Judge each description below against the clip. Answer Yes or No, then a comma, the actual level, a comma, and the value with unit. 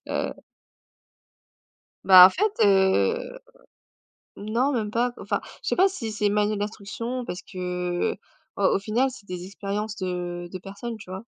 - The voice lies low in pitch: No, high, 205 Hz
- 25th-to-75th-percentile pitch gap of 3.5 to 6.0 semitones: Yes, average, 4.2 semitones